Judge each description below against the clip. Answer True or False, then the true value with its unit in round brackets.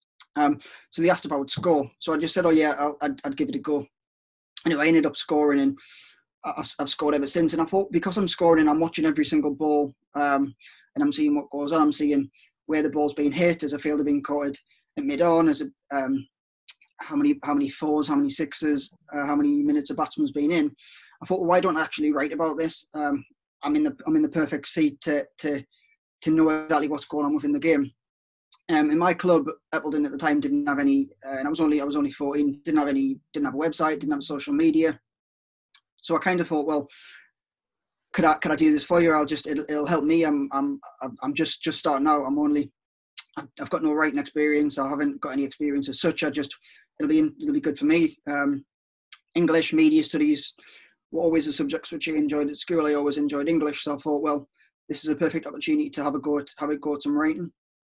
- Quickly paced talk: True (240 wpm)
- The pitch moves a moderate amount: True (3.0 semitones)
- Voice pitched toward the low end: False (150 Hz)